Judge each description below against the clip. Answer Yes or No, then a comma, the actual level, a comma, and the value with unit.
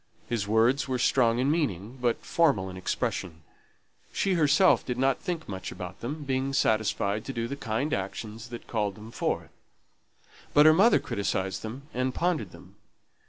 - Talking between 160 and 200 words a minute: Yes, average, 165 wpm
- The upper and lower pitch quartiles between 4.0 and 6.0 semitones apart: Yes, average, 5.0 semitones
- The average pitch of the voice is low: Yes, low, 120 Hz